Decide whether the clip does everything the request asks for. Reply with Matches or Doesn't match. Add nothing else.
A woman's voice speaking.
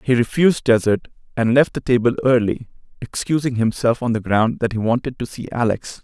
Doesn't match